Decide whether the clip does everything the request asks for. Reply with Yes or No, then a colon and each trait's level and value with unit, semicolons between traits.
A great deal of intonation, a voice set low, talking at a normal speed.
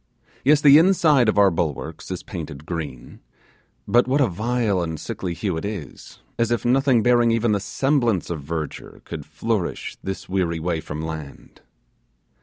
Yes: wide, 6.8 semitones; very low, 95 Hz; average, 165 wpm